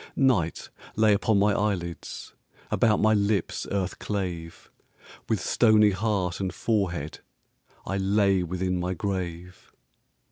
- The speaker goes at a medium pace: No, slow, 115 wpm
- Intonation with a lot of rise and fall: No, average, 2.7 semitones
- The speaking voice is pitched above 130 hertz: No, very low, 95 Hz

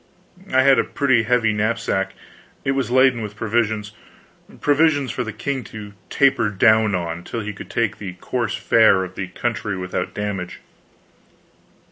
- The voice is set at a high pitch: No, low, 110 Hz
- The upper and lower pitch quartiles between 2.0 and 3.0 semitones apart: No, average, 3.6 semitones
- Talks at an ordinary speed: Yes, average, 160 wpm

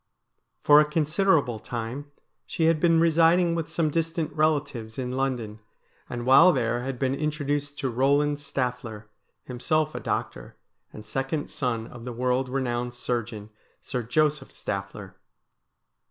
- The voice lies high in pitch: No, low, 135 Hz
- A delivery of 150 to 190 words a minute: No, average, 140 wpm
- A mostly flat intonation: No, average, 4.1 semitones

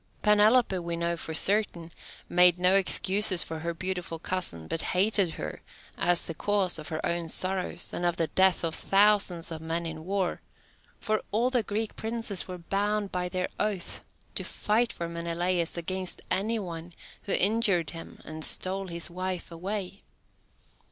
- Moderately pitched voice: Yes, medium, 180 Hz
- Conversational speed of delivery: Yes, average, 165 wpm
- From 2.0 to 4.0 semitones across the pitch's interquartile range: Yes, average, 3.1 semitones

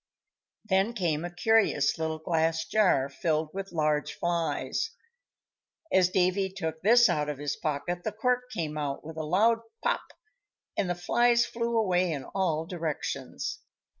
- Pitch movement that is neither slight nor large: Yes, average, 4.5 semitones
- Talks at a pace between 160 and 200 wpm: No, average, 150 wpm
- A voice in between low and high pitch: Yes, medium, 175 Hz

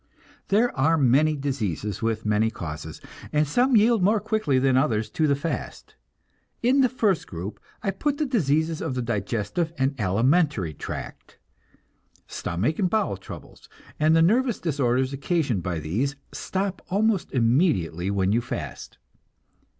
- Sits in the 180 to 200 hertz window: No, medium, 140 Hz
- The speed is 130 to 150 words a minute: Yes, average, 145 wpm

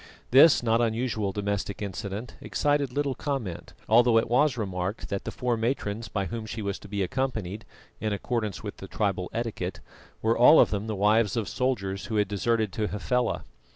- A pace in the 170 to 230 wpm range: Yes, average, 185 wpm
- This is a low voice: Yes, low, 110 Hz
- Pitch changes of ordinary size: Yes, average, 3.0 semitones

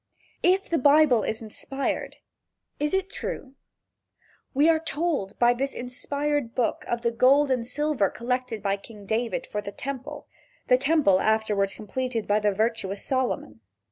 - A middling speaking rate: Yes, average, 150 wpm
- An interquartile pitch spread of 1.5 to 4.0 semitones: No, average, 4.8 semitones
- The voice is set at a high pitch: Yes, very high, 250 Hz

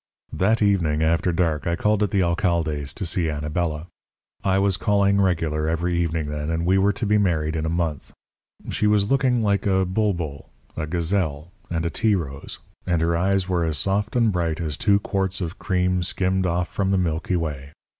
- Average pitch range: Yes, average, 3.4 semitones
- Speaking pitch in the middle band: No, very low, 90 Hz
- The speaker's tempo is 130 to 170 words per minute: No, average, 195 wpm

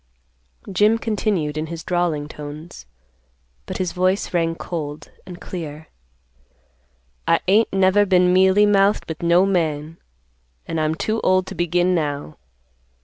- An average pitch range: Yes, average, 3.2 semitones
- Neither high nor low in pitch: Yes, medium, 175 Hz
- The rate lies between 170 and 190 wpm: No, slow, 135 wpm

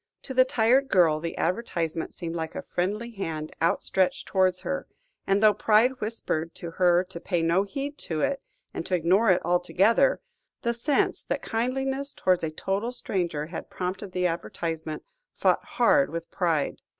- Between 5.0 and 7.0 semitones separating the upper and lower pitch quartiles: Yes, wide, 5.6 semitones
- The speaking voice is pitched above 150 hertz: Yes, medium, 185 Hz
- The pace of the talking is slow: No, average, 165 wpm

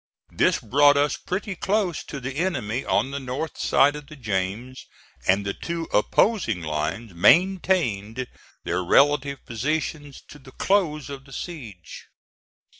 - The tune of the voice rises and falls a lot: Yes, wide, 6.1 semitones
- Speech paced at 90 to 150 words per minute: Yes, average, 140 wpm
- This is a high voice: No, medium, 140 Hz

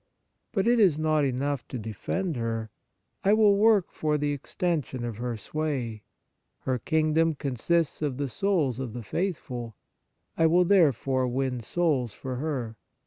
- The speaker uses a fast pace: No, average, 150 wpm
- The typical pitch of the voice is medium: Yes, medium, 145 Hz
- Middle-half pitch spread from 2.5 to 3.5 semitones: No, average, 5.2 semitones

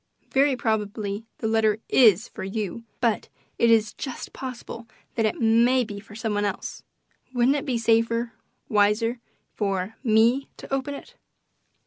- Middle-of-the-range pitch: No, high, 225 Hz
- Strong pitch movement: No, narrow, 2.6 semitones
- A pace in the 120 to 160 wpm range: Yes, average, 150 wpm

